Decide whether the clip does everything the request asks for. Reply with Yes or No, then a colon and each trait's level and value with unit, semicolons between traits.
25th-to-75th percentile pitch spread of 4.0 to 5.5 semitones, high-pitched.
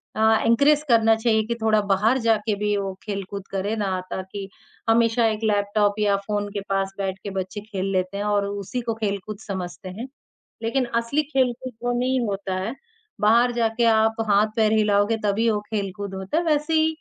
No: narrow, 2.5 semitones; high, 210 Hz